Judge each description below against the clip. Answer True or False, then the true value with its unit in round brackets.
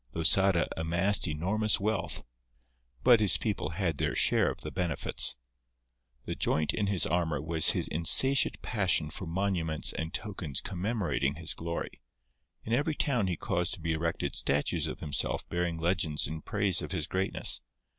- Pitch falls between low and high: False (85 Hz)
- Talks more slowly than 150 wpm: False (155 wpm)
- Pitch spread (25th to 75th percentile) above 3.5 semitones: True (3.9 semitones)